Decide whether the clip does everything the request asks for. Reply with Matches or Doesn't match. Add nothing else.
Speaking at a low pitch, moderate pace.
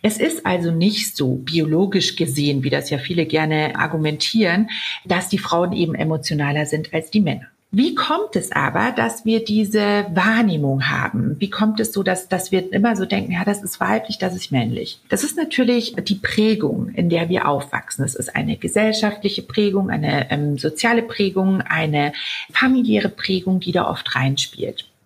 Doesn't match